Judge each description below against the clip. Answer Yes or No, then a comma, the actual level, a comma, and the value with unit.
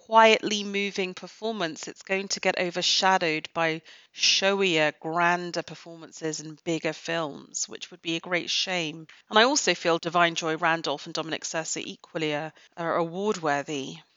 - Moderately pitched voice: Yes, medium, 170 Hz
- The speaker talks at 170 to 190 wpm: No, average, 150 wpm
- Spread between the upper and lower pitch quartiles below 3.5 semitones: Yes, average, 2.8 semitones